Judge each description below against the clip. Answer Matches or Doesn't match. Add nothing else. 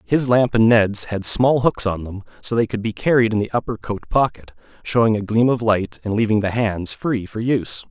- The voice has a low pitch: Matches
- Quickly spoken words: Matches